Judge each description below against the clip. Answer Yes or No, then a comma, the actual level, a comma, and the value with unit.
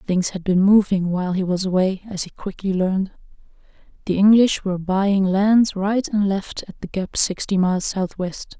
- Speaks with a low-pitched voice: No, high, 190 Hz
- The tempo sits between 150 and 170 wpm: No, average, 180 wpm